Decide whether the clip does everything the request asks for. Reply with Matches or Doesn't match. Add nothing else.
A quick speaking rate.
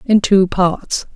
Doesn't match